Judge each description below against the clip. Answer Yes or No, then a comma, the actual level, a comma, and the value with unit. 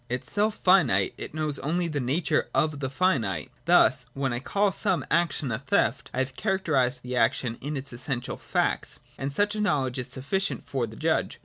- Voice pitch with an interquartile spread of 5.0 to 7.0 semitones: Yes, wide, 5.5 semitones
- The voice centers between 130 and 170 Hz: Yes, medium, 140 Hz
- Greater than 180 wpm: Yes, average, 190 wpm